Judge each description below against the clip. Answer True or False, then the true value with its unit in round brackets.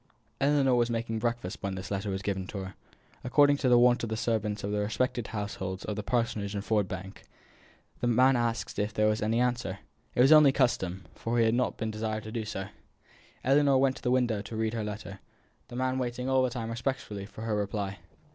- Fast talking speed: True (220 wpm)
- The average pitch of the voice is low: True (110 Hz)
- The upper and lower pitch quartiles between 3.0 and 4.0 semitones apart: True (3.3 semitones)